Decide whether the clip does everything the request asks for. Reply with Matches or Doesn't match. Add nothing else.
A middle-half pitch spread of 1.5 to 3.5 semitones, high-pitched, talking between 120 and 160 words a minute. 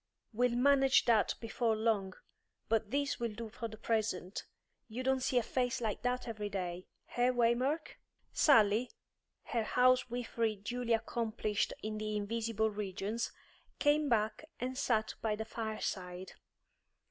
Matches